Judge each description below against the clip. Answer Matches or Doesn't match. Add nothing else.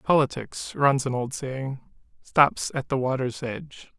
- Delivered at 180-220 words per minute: Doesn't match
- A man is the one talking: Matches